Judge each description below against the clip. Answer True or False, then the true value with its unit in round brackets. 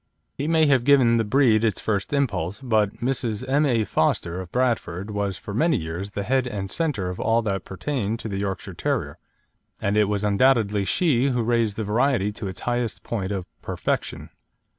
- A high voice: False (110 Hz)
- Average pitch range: True (4.3 semitones)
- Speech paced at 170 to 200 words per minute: True (190 wpm)